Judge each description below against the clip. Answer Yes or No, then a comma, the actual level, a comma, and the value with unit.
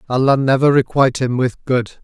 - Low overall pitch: Yes, low, 130 Hz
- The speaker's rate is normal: Yes, average, 175 wpm